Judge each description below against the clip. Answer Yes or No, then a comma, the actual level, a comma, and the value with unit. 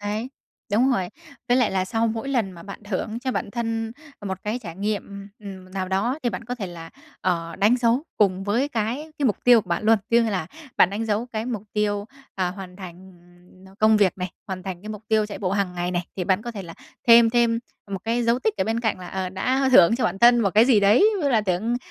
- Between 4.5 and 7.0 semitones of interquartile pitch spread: No, average, 3.7 semitones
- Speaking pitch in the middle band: No, high, 210 Hz